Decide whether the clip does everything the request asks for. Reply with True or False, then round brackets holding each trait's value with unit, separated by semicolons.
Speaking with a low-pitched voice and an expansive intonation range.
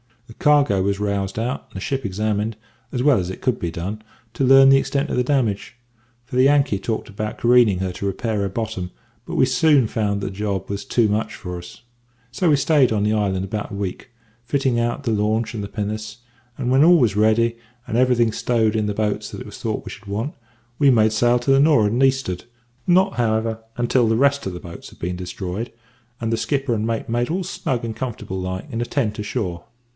False (110 Hz; 3.8 semitones)